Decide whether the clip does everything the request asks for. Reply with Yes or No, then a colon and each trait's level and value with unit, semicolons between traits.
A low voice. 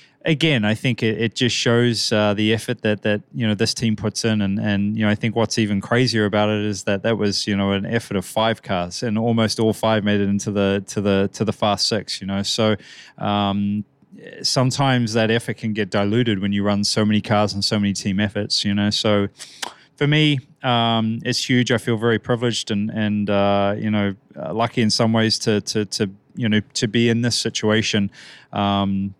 Yes: low, 110 Hz